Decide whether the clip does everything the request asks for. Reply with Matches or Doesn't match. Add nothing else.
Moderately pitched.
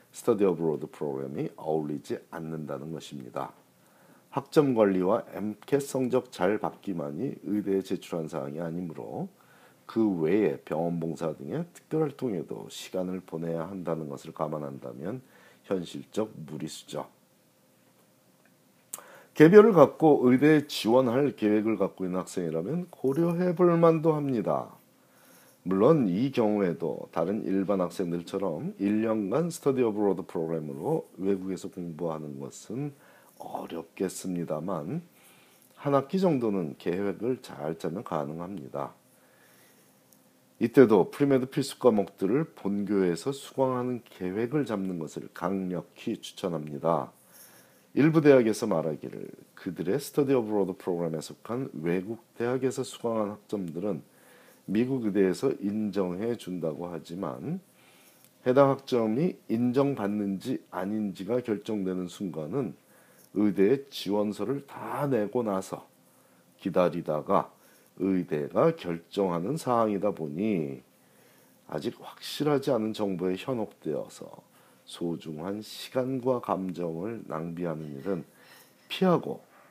Doesn't match